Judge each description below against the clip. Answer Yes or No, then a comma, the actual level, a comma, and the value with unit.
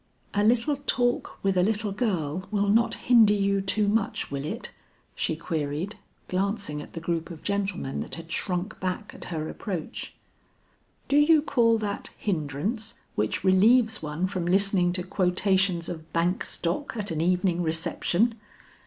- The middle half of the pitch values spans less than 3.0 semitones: No, average, 4.0 semitones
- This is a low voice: No, high, 190 Hz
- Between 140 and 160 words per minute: Yes, average, 155 wpm